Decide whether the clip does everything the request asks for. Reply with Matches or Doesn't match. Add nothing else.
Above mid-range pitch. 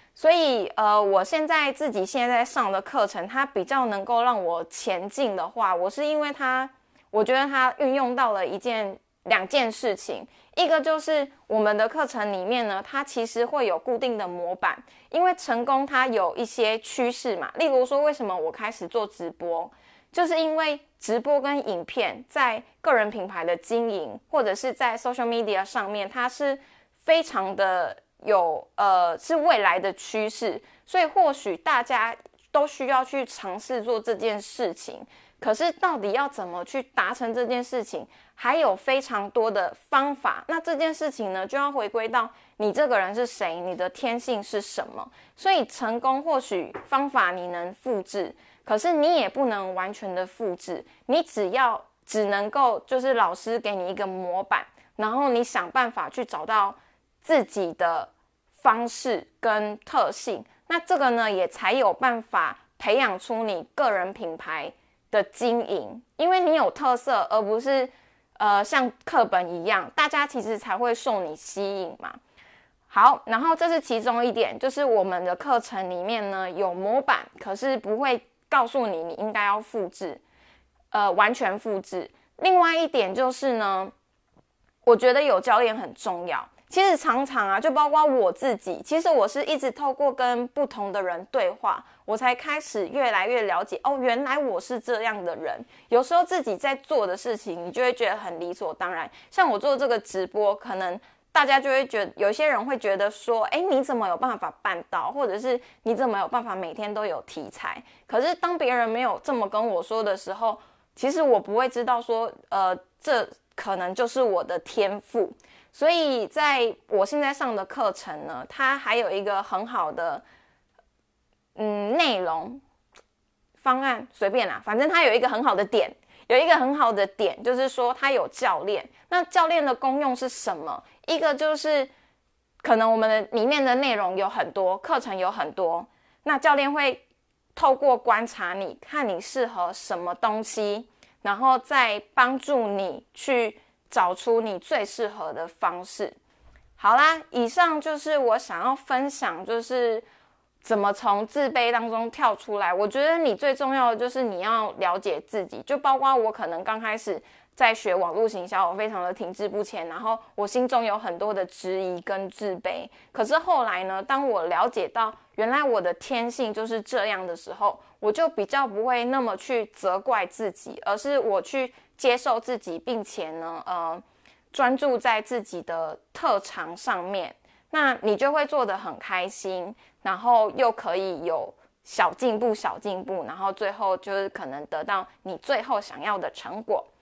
Matches